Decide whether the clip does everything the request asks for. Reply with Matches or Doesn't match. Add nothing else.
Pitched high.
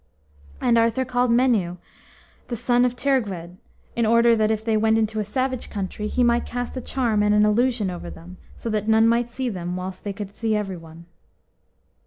Matches